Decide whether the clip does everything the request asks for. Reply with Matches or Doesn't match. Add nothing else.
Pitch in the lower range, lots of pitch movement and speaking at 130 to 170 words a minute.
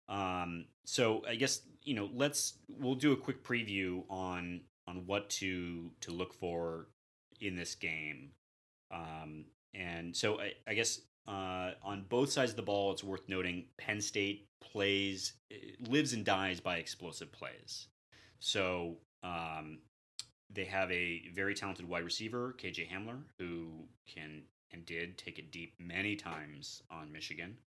Doesn't match